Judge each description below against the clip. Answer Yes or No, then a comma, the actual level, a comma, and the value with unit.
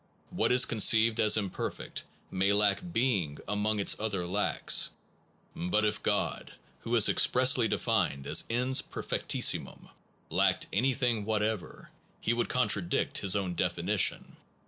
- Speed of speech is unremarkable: No, slow, 130 wpm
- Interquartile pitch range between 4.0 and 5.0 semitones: No, average, 3.0 semitones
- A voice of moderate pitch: No, low, 105 Hz